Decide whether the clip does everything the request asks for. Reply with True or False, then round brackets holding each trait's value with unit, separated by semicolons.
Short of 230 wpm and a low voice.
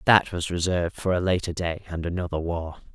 True (205 wpm; 85 Hz)